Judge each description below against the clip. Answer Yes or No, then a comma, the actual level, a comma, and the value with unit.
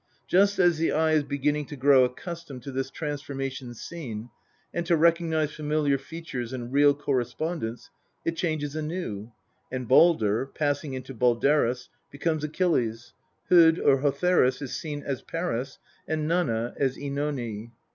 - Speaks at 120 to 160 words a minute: Yes, average, 140 wpm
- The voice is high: No, medium, 145 Hz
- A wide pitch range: No, average, 3.9 semitones